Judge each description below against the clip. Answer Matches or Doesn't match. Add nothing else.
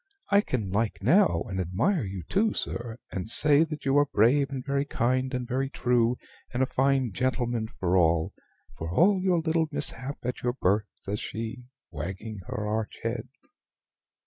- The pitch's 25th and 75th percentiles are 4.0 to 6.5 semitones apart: Matches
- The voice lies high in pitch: Doesn't match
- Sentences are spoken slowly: Doesn't match